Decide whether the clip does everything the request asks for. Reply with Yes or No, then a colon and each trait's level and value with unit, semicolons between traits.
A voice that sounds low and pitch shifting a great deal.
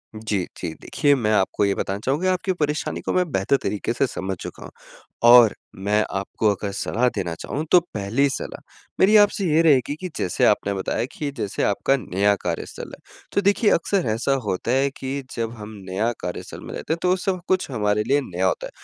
Yes: low, 120 Hz; wide, 7.3 semitones